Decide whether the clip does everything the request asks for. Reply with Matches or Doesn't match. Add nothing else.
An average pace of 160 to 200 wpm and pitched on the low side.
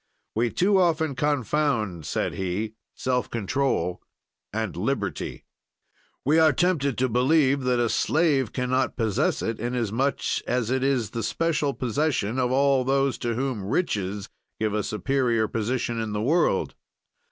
Doesn't match